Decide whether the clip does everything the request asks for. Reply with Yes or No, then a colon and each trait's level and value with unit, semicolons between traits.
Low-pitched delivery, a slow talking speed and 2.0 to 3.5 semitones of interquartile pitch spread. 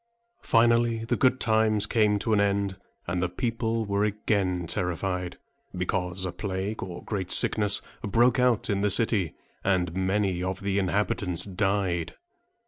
No: low, 100 Hz; average, 145 wpm; average, 3.1 semitones